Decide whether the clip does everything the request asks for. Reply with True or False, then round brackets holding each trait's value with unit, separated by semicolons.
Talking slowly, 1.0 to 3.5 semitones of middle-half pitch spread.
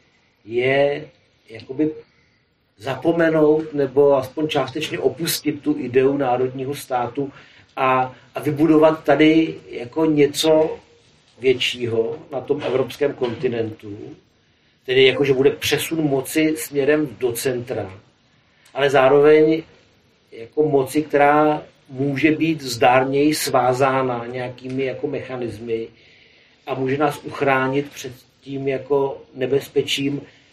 True (100 wpm; 2.9 semitones)